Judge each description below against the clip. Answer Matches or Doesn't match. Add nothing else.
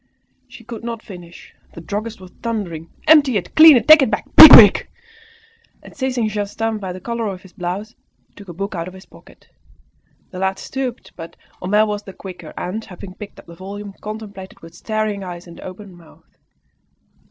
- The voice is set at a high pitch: Matches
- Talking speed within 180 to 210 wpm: Matches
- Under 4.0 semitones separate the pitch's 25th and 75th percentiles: Matches